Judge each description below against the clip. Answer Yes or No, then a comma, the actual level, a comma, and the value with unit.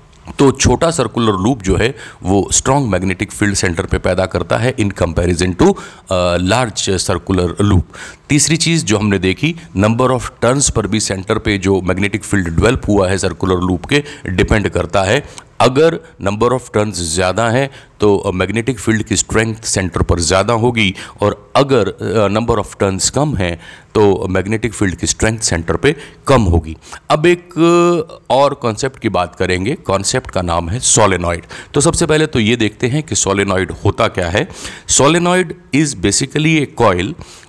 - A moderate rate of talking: Yes, average, 170 wpm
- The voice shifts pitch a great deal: Yes, wide, 5.8 semitones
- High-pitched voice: No, low, 105 Hz